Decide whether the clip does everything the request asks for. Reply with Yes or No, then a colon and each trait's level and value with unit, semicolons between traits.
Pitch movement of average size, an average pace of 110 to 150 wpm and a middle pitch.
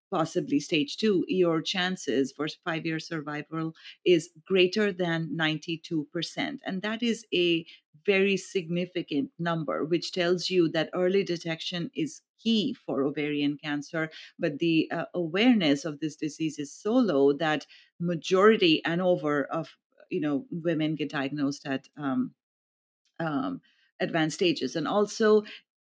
Yes: average, 3.3 semitones; slow, 135 wpm; medium, 165 Hz